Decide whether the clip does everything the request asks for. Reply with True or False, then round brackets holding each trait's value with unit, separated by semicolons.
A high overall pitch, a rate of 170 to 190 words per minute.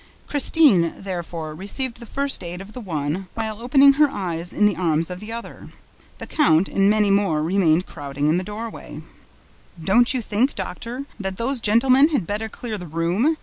True (205 Hz; 185 wpm)